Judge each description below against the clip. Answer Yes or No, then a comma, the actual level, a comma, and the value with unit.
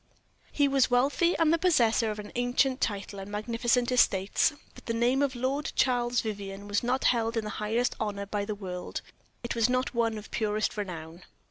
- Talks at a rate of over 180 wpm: Yes, average, 190 wpm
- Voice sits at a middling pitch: No, high, 230 Hz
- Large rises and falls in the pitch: No, average, 3.4 semitones